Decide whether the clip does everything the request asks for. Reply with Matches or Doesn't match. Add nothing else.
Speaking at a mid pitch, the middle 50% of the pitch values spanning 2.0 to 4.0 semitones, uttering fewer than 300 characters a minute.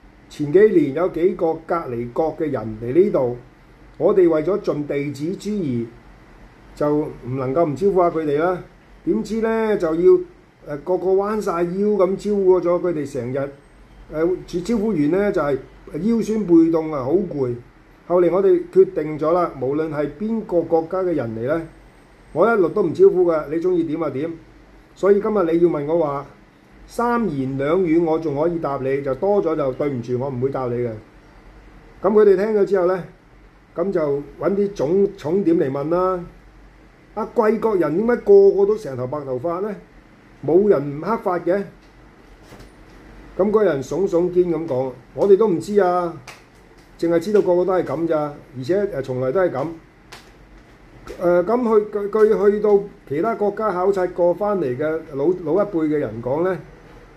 Doesn't match